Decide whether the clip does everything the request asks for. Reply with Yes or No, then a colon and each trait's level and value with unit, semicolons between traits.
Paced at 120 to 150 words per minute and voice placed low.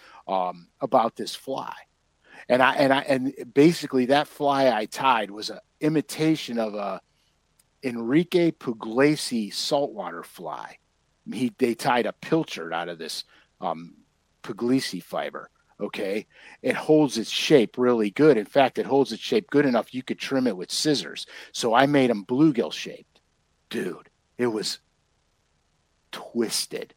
Yes: average, 145 wpm; low, 125 Hz